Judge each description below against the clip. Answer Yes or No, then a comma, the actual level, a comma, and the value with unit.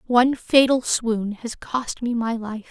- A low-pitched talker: No, high, 235 Hz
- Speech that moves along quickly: No, average, 175 wpm